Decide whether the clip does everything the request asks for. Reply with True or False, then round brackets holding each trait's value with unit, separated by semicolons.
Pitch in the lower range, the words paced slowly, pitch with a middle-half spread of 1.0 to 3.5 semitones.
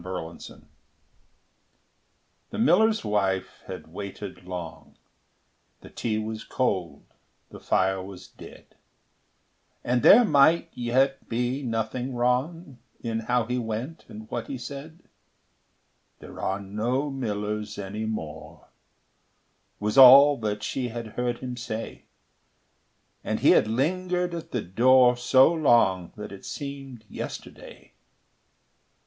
False (120 Hz; 120 wpm; 4.4 semitones)